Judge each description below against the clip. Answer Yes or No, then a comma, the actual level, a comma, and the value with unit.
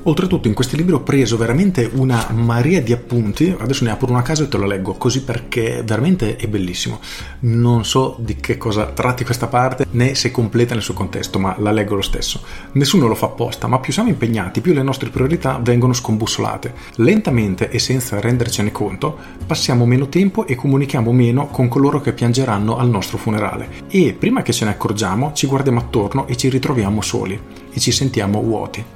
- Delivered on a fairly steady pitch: No, average, 3.4 semitones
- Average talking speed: No, fast, 195 wpm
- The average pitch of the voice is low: Yes, low, 120 Hz